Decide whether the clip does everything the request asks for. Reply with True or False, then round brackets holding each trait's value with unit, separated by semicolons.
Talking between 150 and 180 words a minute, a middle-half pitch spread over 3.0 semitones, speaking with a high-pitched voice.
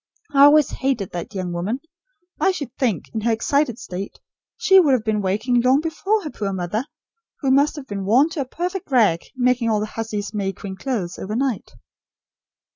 False (190 wpm; 5.5 semitones; 235 Hz)